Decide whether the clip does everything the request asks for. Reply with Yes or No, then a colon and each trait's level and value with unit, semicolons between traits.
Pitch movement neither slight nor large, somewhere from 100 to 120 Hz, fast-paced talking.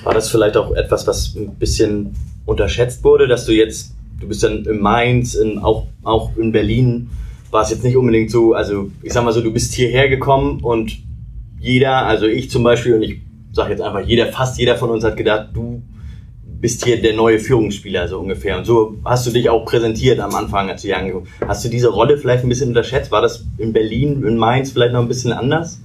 No: narrow, 2.1 semitones; low, 115 Hz; fast, 220 wpm